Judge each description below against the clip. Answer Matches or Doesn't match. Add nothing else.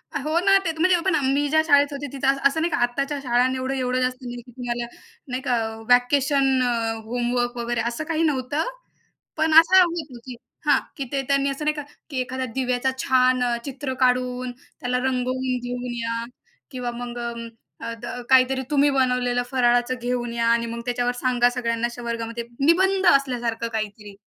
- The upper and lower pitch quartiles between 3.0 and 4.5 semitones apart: Doesn't match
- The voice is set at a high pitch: Matches